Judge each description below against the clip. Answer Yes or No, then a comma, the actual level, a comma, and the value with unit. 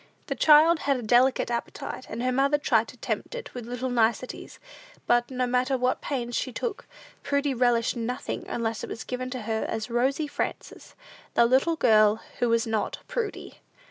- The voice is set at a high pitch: Yes, very high, 250 Hz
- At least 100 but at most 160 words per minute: No, average, 180 wpm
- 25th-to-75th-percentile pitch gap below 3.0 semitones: Yes, narrow, 2.6 semitones